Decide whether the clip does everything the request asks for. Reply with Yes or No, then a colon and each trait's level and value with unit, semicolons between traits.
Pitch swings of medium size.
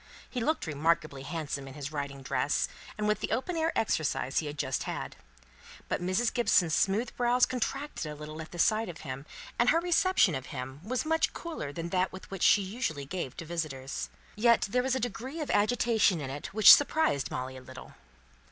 No: wide, 9.0 semitones